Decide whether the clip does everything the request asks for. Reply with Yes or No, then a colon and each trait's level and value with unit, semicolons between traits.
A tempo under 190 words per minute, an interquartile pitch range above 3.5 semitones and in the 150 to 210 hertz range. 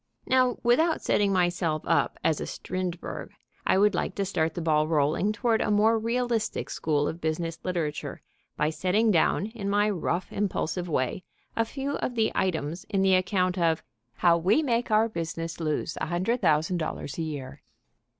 Yes: average, 165 wpm; average, 4.9 semitones; medium, 185 Hz